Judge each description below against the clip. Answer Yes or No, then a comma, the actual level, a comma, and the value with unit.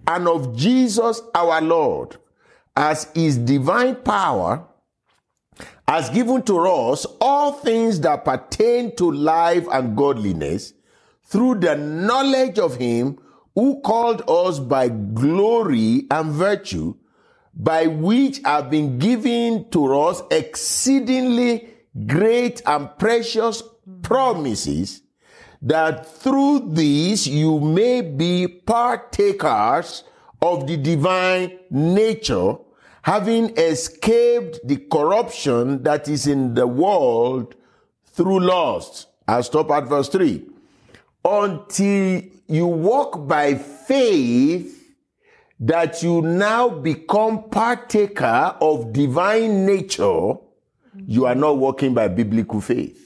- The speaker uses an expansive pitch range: Yes, wide, 7.6 semitones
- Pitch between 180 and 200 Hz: Yes, medium, 185 Hz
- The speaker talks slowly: Yes, slow, 105 wpm